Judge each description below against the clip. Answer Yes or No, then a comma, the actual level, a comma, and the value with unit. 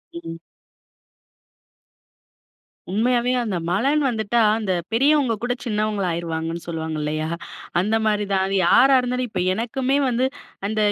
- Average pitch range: No, wide, 5.9 semitones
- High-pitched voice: Yes, high, 215 Hz